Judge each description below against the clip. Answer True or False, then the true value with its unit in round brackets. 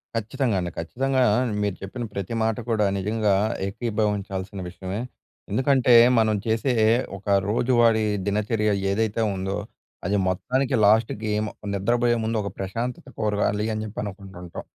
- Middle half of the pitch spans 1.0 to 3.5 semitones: True (2.7 semitones)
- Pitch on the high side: False (105 Hz)